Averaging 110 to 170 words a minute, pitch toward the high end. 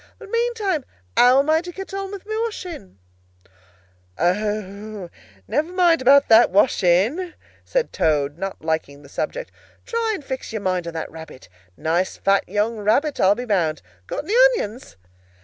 Yes: average, 165 wpm; high, 225 Hz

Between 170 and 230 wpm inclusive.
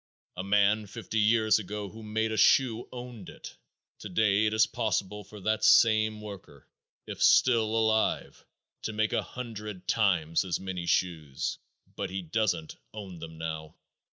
No: average, 155 wpm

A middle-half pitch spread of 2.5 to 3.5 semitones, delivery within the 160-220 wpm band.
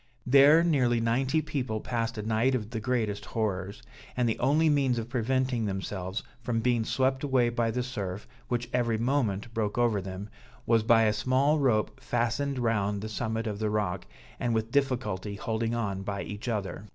Yes: average, 3.1 semitones; average, 180 wpm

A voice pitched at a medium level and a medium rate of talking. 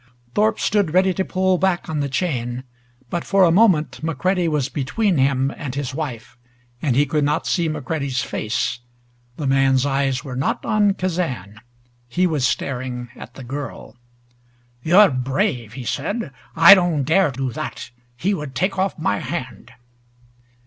Yes: medium, 145 Hz; average, 160 wpm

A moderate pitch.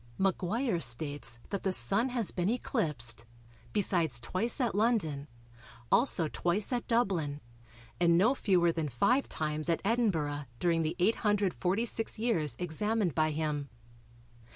Yes: medium, 175 Hz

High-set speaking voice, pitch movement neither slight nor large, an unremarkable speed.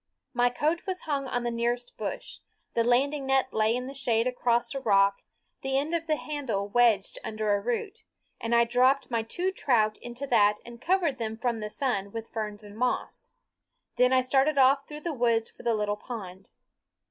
Yes: high, 245 Hz; average, 3.5 semitones; average, 195 wpm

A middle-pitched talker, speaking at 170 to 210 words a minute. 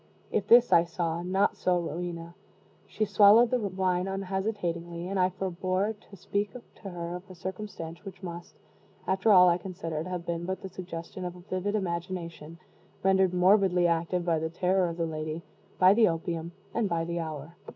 Yes: medium, 180 Hz; average, 180 wpm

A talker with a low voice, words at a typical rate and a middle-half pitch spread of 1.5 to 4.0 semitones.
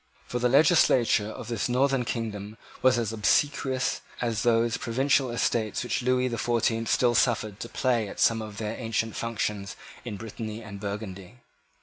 Yes: low, 115 Hz; average, 160 wpm; narrow, 2.4 semitones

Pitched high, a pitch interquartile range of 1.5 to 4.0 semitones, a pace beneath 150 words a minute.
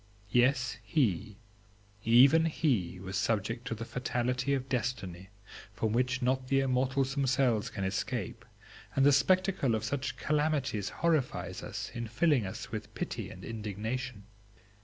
No: low, 125 Hz; average, 3.7 semitones; slow, 135 wpm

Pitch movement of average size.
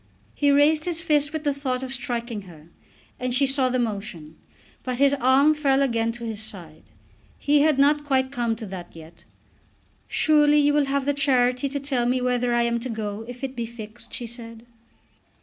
Yes: average, 3.5 semitones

